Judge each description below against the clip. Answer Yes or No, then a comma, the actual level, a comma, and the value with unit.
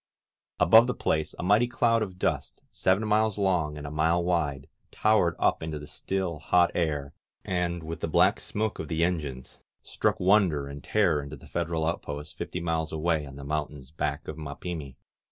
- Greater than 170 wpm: Yes, average, 195 wpm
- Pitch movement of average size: Yes, average, 3.5 semitones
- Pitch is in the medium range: No, very low, 80 Hz